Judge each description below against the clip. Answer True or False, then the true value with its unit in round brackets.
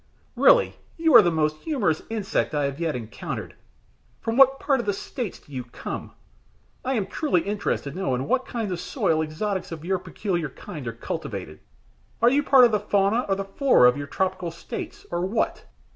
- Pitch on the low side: False (190 Hz)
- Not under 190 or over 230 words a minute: True (200 wpm)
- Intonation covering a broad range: True (7.2 semitones)